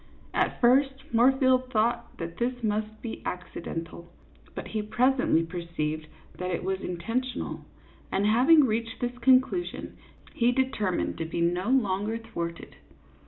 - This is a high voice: Yes, high, 225 Hz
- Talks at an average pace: No, slow, 130 wpm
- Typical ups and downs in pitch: No, wide, 6.0 semitones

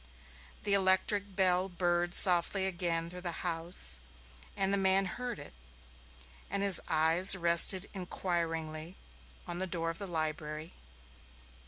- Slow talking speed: Yes, slow, 130 wpm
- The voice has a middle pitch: Yes, medium, 175 Hz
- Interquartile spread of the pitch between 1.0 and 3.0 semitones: Yes, narrow, 2.4 semitones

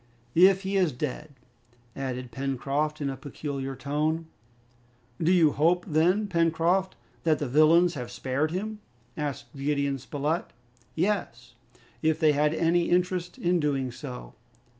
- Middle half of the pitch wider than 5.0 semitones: No, average, 4.0 semitones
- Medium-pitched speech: Yes, medium, 155 Hz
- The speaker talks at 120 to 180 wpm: Yes, slow, 135 wpm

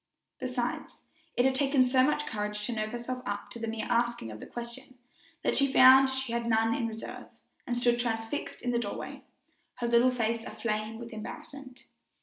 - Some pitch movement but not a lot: No, narrow, 2.3 semitones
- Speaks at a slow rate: No, average, 185 wpm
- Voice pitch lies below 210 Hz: No, high, 240 Hz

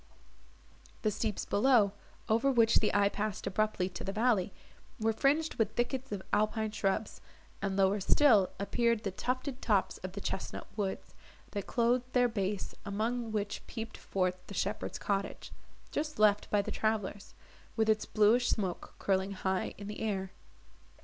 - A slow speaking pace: No, average, 155 wpm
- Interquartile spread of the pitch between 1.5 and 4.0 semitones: Yes, average, 2.7 semitones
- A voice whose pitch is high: Yes, high, 215 Hz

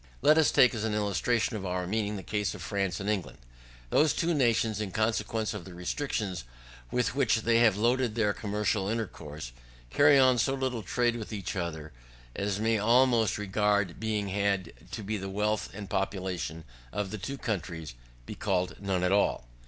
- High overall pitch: No, low, 105 Hz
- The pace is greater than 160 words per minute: Yes, average, 180 wpm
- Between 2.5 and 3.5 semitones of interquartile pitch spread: Yes, average, 3.1 semitones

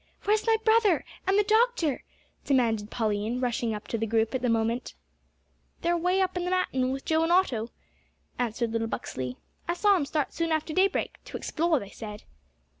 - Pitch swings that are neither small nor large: No, wide, 8.2 semitones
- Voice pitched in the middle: No, very high, 275 Hz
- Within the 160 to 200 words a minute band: Yes, average, 190 wpm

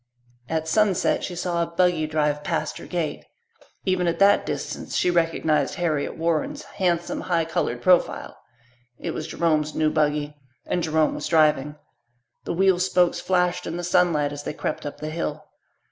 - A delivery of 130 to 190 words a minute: Yes, average, 165 wpm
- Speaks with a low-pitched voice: No, medium, 165 Hz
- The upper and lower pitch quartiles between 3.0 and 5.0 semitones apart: No, narrow, 2.5 semitones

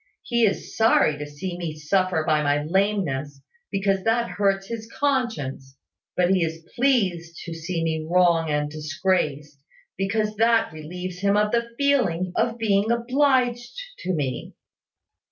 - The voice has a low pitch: No, medium, 185 Hz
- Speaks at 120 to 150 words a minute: Yes, average, 145 wpm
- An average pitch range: No, wide, 6.1 semitones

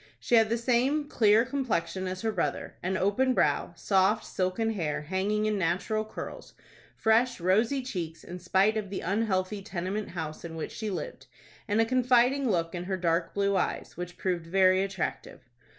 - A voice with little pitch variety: No, average, 3.7 semitones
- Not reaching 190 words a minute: Yes, average, 175 wpm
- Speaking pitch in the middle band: No, high, 195 Hz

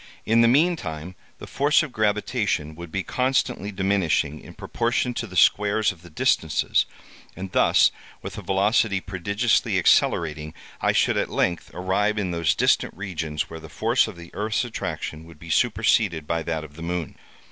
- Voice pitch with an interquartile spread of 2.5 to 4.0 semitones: No, average, 4.9 semitones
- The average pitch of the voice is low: Yes, very low, 95 Hz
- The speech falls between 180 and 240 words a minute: No, average, 170 wpm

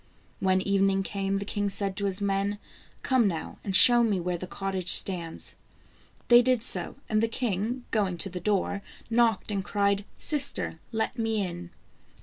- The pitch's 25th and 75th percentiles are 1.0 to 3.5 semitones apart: Yes, average, 2.7 semitones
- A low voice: No, high, 200 Hz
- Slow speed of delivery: No, average, 180 wpm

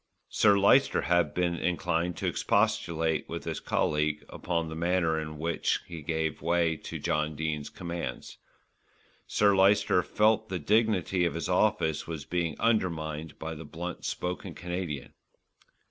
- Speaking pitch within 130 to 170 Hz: No, very low, 85 Hz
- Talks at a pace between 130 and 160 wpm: Yes, average, 145 wpm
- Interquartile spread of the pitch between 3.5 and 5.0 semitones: No, narrow, 2.5 semitones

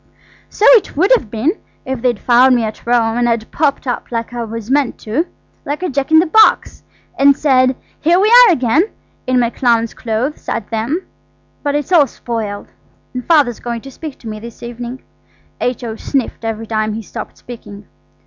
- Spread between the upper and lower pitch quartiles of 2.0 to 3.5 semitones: No, average, 4.2 semitones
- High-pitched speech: Yes, high, 245 Hz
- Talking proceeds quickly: No, average, 185 wpm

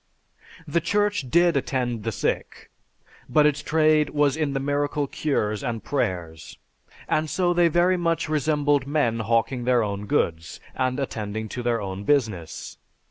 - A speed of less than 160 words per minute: Yes, average, 150 wpm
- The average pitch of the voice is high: No, low, 135 Hz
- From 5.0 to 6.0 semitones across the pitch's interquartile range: Yes, wide, 5.4 semitones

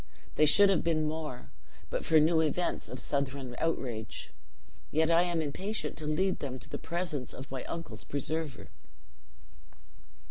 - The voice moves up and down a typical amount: Yes, average, 3.7 semitones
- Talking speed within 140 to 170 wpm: Yes, average, 150 wpm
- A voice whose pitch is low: No, medium, 155 Hz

